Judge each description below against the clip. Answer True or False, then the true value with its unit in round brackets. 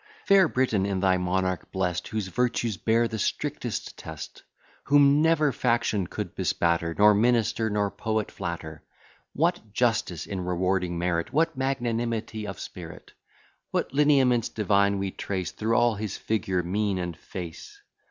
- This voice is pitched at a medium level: False (105 Hz)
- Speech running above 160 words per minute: False (145 wpm)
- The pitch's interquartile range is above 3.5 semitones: True (4.5 semitones)